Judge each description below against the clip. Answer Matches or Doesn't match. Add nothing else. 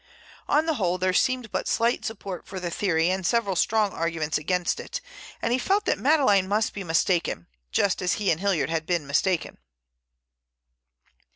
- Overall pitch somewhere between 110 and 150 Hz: Doesn't match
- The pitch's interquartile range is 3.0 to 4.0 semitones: Doesn't match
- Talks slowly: Doesn't match